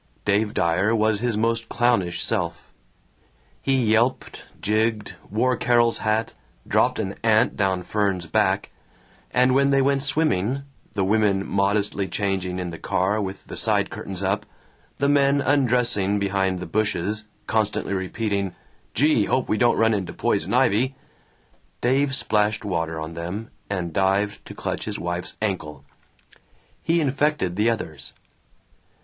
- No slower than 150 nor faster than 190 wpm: No, average, 140 wpm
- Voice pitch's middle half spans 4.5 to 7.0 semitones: No, average, 4.0 semitones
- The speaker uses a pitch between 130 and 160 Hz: No, low, 105 Hz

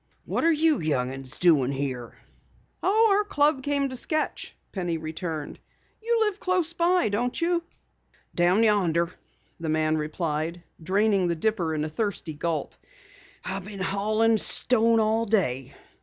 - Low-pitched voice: No, high, 200 Hz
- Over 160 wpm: No, average, 145 wpm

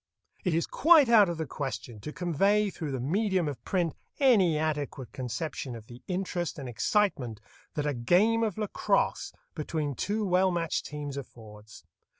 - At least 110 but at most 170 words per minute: Yes, average, 160 wpm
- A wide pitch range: Yes, wide, 6.3 semitones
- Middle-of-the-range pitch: Yes, medium, 160 Hz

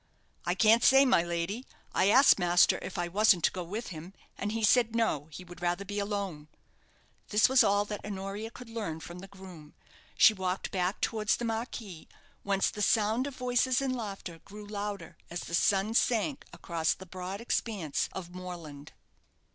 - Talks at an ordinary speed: Yes, average, 180 wpm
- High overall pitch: Yes, high, 200 Hz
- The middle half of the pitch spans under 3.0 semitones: No, average, 4.1 semitones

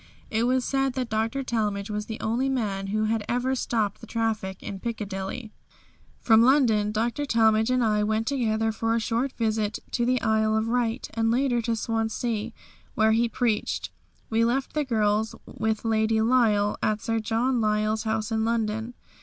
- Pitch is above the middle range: Yes, high, 225 Hz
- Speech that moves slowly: No, average, 175 wpm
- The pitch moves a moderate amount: No, narrow, 1.7 semitones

